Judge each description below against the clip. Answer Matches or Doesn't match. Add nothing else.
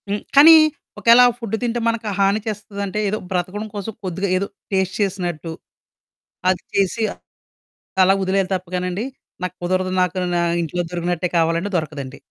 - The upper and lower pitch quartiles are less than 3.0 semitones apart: Matches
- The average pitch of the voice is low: Doesn't match